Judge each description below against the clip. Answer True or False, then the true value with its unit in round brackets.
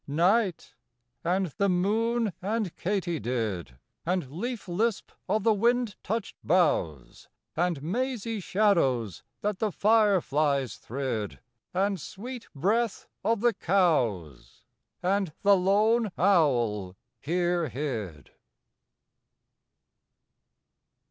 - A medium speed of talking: False (95 wpm)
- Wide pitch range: True (7.2 semitones)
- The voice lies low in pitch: False (185 Hz)